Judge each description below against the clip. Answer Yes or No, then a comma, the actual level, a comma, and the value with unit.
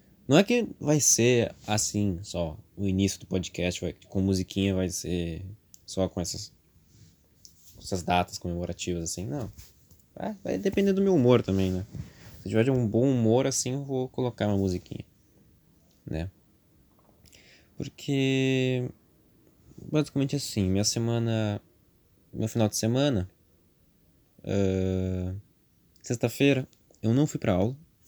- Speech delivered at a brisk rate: No, average, 130 wpm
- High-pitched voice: No, low, 100 Hz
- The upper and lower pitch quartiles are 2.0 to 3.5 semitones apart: No, average, 5.3 semitones